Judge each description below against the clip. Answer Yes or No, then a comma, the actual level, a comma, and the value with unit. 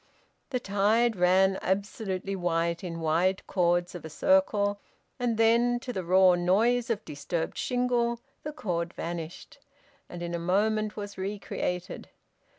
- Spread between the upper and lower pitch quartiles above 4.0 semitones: Yes, average, 4.4 semitones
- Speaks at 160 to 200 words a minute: No, average, 150 wpm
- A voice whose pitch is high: Yes, high, 195 Hz